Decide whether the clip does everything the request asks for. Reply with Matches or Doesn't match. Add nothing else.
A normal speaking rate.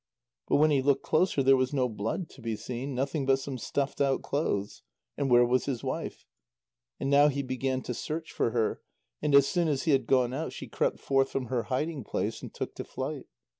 Doesn't match